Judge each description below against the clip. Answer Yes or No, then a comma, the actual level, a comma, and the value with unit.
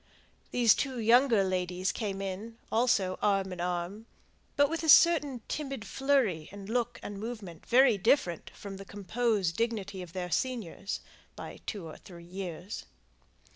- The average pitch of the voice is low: No, high, 205 Hz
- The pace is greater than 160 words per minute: No, average, 150 wpm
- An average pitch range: Yes, average, 4.6 semitones